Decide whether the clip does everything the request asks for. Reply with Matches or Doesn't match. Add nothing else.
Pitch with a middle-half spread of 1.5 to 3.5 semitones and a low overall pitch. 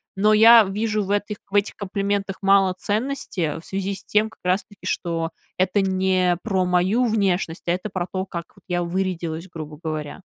Doesn't match